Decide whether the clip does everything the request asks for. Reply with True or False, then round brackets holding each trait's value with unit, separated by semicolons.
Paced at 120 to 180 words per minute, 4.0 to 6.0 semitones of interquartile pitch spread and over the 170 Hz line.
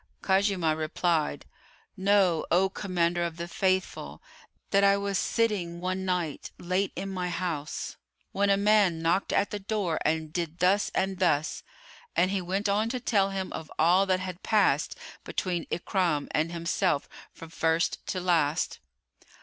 False (155 wpm; 2.8 semitones; 185 Hz)